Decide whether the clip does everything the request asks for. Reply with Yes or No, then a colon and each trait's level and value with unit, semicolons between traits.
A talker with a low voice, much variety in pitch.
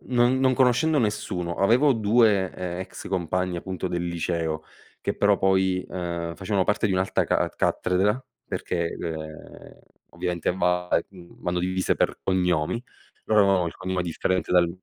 No: very low, 95 Hz; average, 2.7 semitones